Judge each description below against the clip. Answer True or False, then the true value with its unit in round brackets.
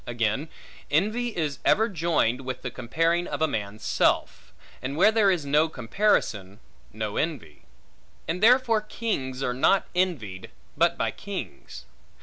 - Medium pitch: True (150 Hz)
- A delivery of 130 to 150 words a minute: True (140 wpm)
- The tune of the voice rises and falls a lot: True (8.0 semitones)